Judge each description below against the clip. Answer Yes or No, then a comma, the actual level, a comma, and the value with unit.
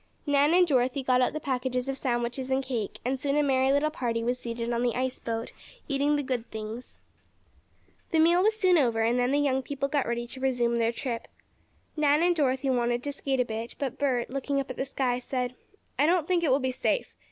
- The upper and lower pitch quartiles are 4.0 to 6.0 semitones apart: No, average, 2.8 semitones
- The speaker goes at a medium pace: No, fast, 230 wpm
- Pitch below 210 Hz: No, very high, 260 Hz